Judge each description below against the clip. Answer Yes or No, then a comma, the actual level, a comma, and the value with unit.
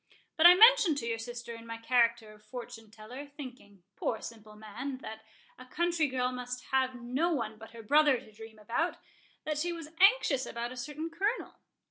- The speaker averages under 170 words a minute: No, average, 180 wpm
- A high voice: Yes, very high, 250 Hz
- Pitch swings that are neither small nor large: Yes, average, 5.0 semitones